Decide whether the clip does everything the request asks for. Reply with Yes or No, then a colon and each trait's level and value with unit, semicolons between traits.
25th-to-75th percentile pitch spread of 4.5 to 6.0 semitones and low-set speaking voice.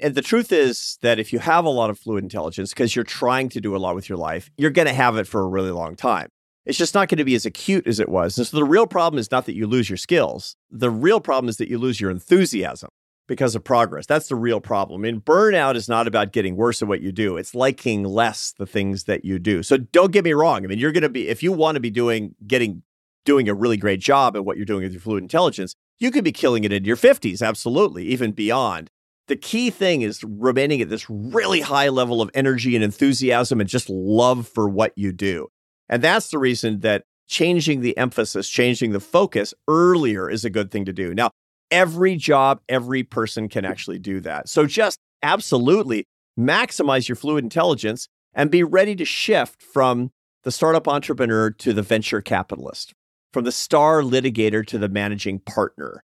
Yes: average, 4.9 semitones; low, 120 Hz